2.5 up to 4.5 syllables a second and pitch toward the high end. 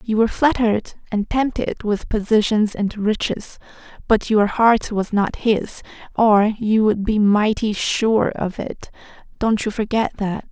Yes: 4.1 syllables/s; high, 215 Hz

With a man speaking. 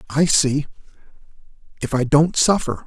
Yes: male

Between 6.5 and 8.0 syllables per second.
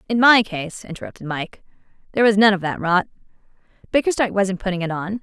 Yes: 6.6 syllables/s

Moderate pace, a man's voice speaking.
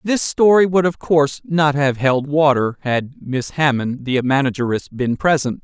Yes: average, 170 wpm; male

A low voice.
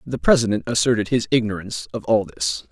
Yes: low, 115 Hz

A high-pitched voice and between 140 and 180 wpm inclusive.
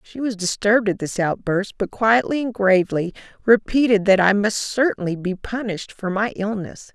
Yes: high, 205 Hz; average, 175 wpm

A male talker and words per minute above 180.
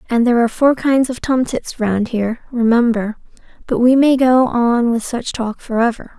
No: female; average, 195 wpm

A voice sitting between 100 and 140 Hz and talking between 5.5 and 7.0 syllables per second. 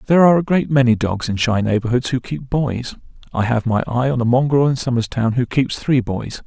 Yes: low, 125 Hz; 5.6 syllables/s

